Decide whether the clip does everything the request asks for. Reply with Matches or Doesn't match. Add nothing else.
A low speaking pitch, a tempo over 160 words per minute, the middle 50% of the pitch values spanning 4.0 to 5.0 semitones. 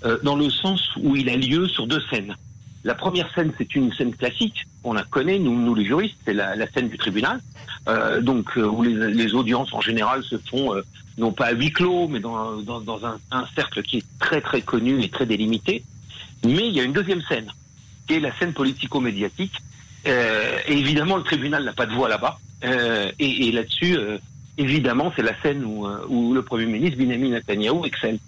Matches